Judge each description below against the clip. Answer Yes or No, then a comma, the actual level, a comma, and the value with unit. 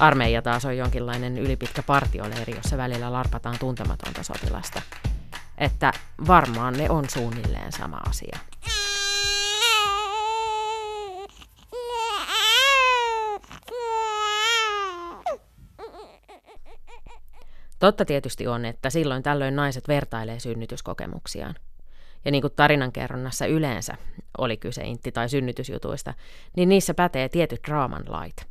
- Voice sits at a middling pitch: Yes, medium, 145 Hz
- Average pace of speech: No, slow, 90 wpm